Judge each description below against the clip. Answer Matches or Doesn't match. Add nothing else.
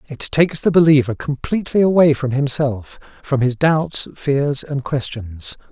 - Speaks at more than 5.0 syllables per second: Doesn't match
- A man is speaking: Matches